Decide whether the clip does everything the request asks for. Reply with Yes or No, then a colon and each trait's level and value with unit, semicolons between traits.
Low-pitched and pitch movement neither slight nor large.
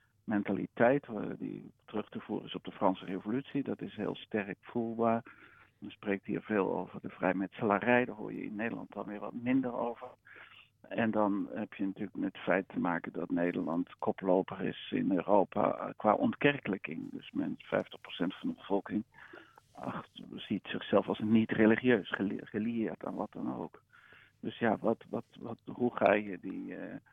Yes: low, 110 Hz; average, 3.6 semitones